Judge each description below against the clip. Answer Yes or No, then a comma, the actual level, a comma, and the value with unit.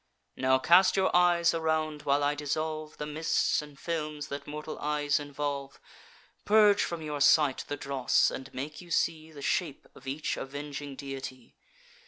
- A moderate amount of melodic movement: No, narrow, 2.0 semitones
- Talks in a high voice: No, medium, 150 Hz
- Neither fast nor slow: Yes, average, 160 wpm